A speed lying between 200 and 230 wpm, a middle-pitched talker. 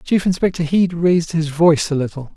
Yes: fast, 205 wpm; medium, 165 Hz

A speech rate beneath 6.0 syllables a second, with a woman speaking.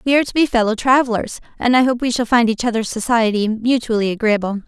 No: 6.5 syllables/s; female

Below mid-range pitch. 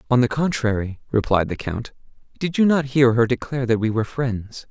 Yes: low, 125 Hz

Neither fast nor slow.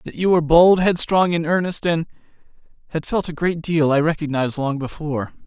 Yes: average, 185 wpm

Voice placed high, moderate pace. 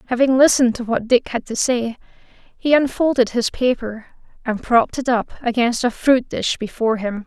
Yes: high, 240 Hz; average, 180 wpm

